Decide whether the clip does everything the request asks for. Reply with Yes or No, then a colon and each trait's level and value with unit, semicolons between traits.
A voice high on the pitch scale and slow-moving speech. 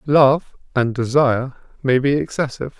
No: low, 135 Hz; slow, 130 wpm